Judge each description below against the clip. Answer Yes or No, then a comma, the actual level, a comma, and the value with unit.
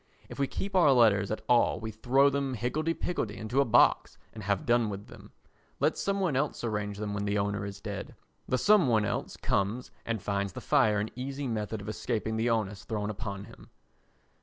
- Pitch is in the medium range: No, low, 110 Hz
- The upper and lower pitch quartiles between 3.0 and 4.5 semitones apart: Yes, average, 3.9 semitones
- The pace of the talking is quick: Yes, fast, 210 wpm